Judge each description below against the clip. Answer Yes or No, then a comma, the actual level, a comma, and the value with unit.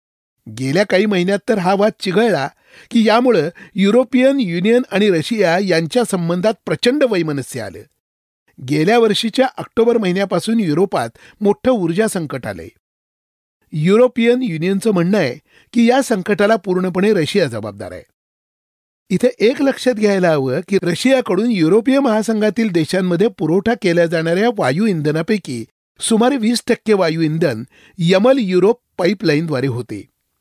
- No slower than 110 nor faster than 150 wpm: Yes, average, 120 wpm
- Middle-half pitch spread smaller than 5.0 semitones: No, wide, 5.6 semitones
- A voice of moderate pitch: No, high, 195 Hz